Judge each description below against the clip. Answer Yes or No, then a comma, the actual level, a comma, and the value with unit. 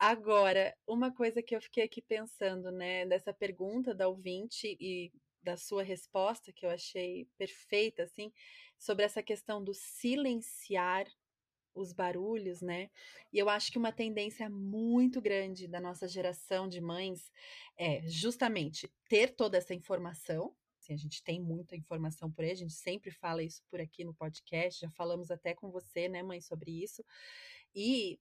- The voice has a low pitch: No, high, 190 Hz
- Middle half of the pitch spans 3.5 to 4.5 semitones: Yes, average, 3.9 semitones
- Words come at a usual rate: Yes, average, 160 wpm